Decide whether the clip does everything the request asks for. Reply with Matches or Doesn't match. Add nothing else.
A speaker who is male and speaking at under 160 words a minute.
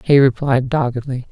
Doesn't match